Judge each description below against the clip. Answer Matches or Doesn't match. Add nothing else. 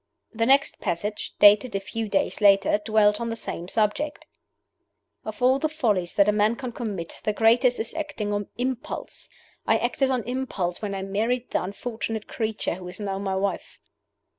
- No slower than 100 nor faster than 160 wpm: Doesn't match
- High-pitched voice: Matches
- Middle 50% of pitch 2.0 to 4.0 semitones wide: Matches